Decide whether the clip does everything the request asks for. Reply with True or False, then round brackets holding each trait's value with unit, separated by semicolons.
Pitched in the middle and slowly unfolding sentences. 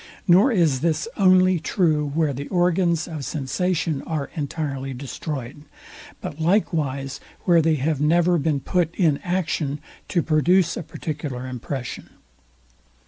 True (160 Hz; 130 wpm)